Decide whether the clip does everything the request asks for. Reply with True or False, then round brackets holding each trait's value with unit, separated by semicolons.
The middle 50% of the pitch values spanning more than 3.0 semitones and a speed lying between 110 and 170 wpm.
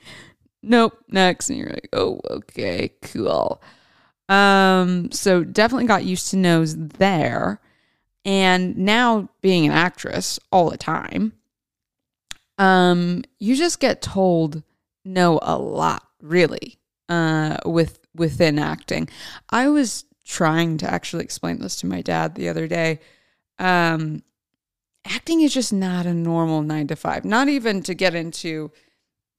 True (4.8 semitones; 135 wpm)